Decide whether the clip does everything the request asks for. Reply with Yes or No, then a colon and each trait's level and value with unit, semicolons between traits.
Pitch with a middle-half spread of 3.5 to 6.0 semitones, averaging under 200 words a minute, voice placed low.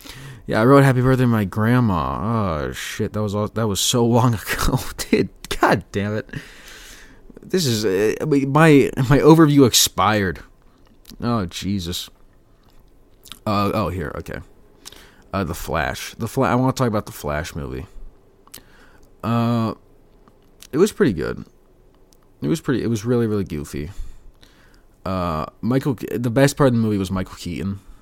Yes: average, 5.3 semitones; average, 155 wpm; low, 110 Hz